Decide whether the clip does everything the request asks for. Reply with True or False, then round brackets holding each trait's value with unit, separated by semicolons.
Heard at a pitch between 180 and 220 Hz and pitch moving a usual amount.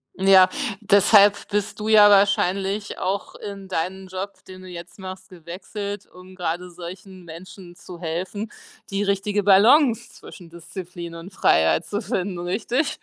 False (190 Hz; 2.3 semitones)